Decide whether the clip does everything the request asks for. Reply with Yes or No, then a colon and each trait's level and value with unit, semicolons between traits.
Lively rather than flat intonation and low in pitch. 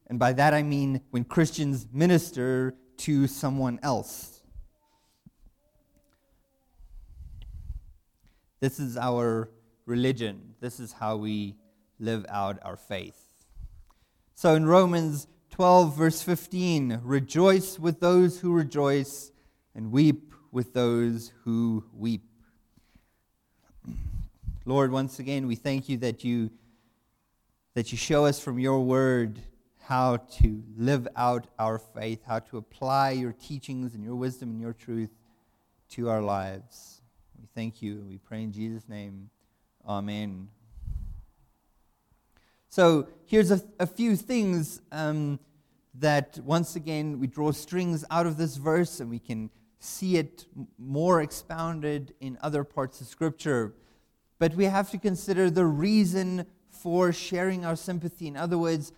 Yes: wide, 6.1 semitones; low, 130 Hz